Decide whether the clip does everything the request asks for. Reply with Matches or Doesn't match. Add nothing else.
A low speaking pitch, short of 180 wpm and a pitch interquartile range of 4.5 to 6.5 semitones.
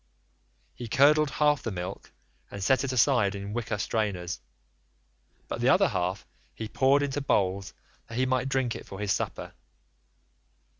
Matches